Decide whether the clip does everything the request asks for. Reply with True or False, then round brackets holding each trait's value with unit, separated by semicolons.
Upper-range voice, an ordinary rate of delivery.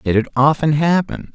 False (150 Hz; 180 wpm)